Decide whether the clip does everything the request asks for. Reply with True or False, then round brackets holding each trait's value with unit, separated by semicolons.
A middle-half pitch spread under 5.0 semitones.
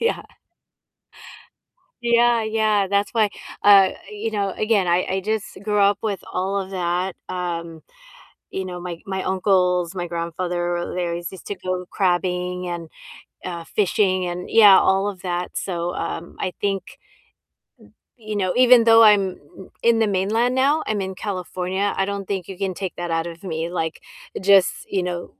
True (2.5 semitones)